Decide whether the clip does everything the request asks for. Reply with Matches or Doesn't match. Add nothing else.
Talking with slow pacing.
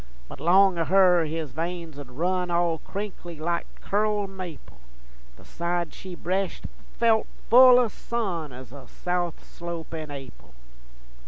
Doesn't match